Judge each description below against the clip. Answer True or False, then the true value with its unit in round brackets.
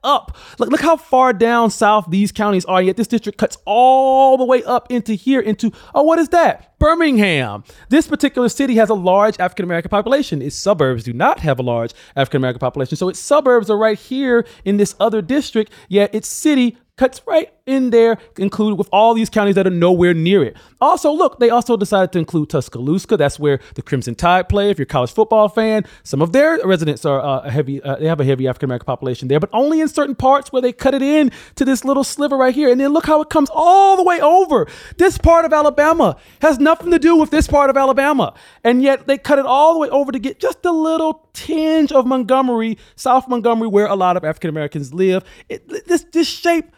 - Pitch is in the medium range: False (235 Hz)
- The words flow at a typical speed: False (230 wpm)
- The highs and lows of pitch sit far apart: True (7.7 semitones)